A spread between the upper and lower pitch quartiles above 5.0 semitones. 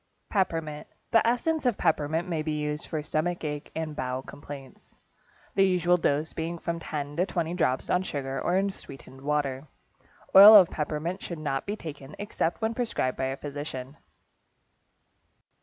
No: average, 3.8 semitones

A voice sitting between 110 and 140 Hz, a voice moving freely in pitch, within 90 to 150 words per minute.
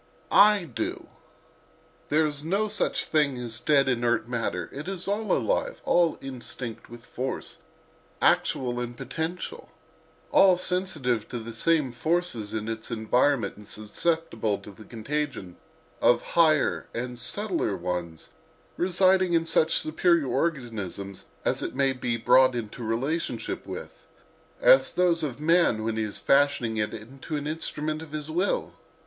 Yes: low, 135 Hz; wide, 6.4 semitones; average, 140 wpm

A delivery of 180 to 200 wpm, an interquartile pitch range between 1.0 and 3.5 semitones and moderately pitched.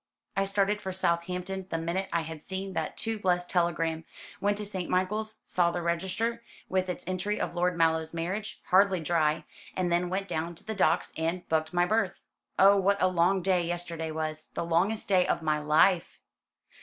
Yes: average, 190 wpm; narrow, 2.6 semitones; medium, 180 Hz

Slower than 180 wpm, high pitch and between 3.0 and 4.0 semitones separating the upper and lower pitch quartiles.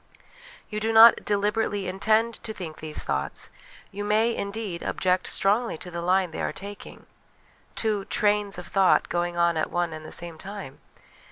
Yes: average, 170 wpm; high, 195 Hz; average, 3.4 semitones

